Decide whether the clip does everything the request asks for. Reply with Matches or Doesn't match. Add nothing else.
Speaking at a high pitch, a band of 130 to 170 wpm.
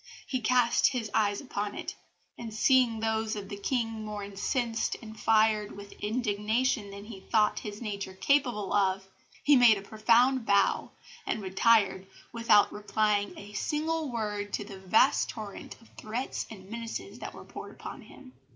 Matches